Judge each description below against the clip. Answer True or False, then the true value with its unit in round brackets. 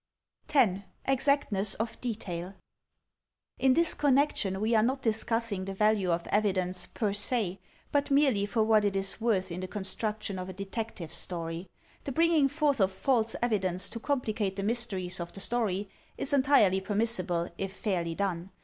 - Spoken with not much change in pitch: False (4.1 semitones)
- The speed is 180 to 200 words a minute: False (165 wpm)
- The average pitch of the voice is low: False (205 Hz)